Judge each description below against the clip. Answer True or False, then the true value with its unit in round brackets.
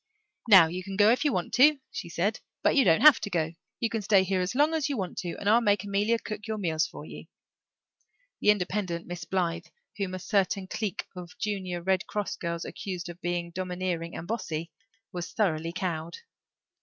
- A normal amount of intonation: True (3.3 semitones)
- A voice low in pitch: False (185 Hz)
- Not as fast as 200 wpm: False (205 wpm)